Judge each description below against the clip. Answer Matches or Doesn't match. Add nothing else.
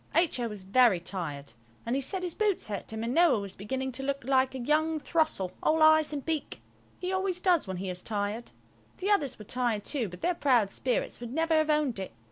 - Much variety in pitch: Matches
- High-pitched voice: Matches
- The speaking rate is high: Matches